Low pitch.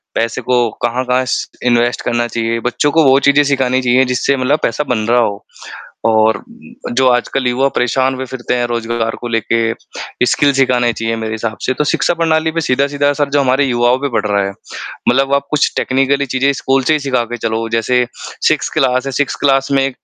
Yes: low, 125 Hz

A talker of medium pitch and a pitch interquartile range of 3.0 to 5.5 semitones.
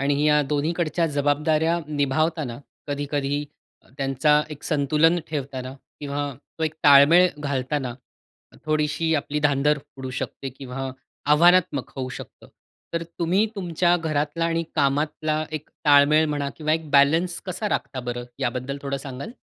No: medium, 150 Hz; narrow, 2.4 semitones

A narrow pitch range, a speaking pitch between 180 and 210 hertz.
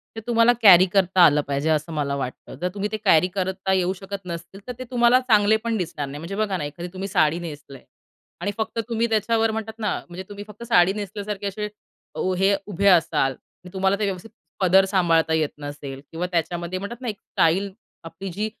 No: average, 3.9 semitones; high, 190 Hz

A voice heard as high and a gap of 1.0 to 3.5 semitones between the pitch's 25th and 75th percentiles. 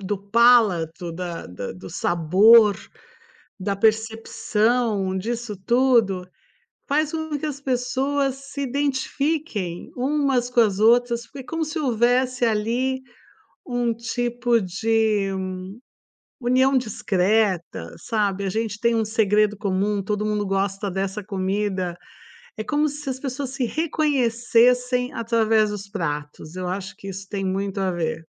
No: high, 225 Hz; average, 4.3 semitones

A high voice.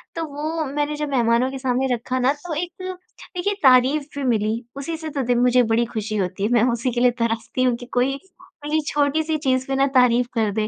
Yes: very high, 255 Hz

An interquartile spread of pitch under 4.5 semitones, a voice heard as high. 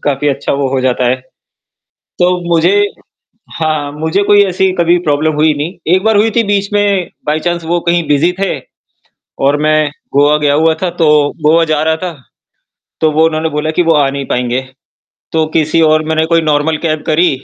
No: average, 2.9 semitones; medium, 160 Hz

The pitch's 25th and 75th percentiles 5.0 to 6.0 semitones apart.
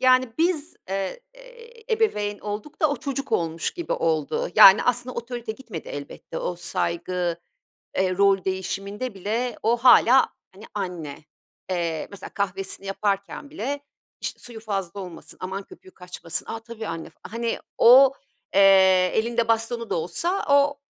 Yes: average, 5.3 semitones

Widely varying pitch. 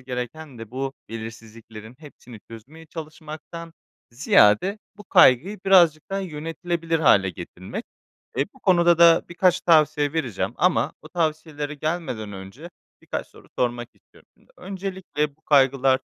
Yes: wide, 5.7 semitones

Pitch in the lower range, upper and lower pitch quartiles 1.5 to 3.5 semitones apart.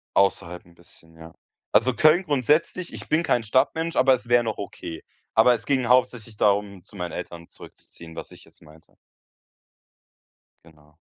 No: low, 110 Hz; wide, 7.2 semitones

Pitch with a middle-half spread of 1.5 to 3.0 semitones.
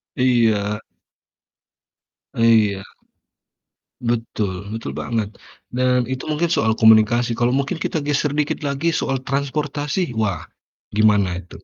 No: average, 4.5 semitones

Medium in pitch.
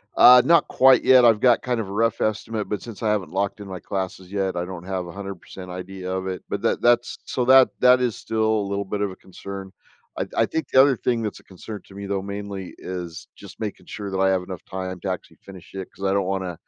No: low, 100 Hz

